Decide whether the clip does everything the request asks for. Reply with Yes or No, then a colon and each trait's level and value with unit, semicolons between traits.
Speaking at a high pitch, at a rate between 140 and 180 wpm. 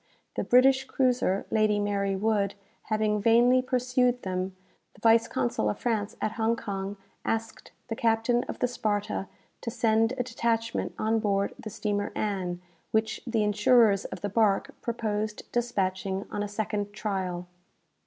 Yes: high, 215 Hz; average, 150 wpm